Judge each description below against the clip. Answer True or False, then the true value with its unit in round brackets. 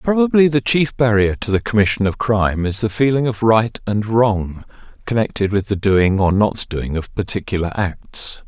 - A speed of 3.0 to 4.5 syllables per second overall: False (4.8 syllables/s)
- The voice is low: True (110 Hz)